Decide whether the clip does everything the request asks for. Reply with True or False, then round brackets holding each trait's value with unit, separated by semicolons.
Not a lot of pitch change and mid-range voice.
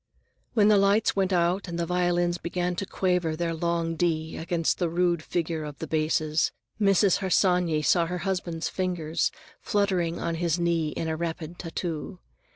True (1.8 semitones; 170 Hz)